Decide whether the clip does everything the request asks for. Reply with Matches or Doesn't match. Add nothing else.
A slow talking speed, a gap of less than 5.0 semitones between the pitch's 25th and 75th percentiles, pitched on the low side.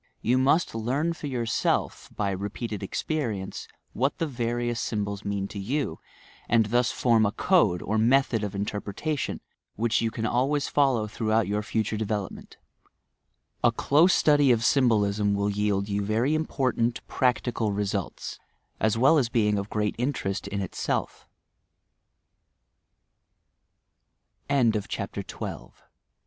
Matches